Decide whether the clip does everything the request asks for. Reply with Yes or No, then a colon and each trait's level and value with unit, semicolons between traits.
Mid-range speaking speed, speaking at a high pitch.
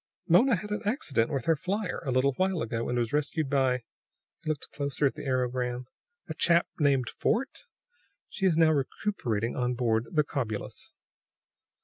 No: average, 170 wpm; medium, 140 Hz